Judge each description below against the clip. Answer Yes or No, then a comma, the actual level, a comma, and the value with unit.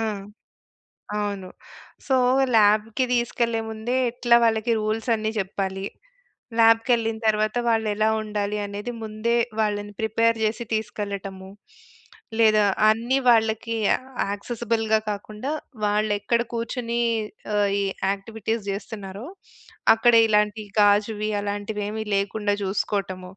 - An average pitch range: No, narrow, 1.7 semitones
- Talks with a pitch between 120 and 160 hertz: No, high, 215 Hz